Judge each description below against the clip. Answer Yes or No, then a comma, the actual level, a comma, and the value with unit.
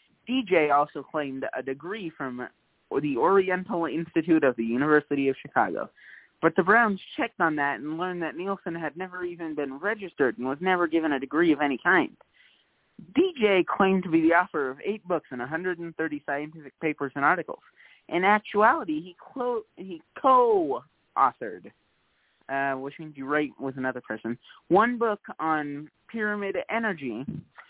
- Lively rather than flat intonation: Yes, wide, 5.9 semitones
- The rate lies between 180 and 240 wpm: No, average, 150 wpm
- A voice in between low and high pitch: Yes, medium, 165 Hz